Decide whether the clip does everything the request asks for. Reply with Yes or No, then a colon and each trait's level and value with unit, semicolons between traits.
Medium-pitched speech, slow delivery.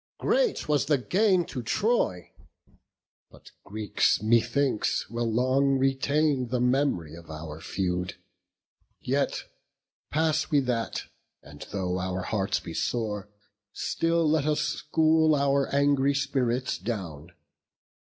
No: low, 130 Hz; slow, 115 wpm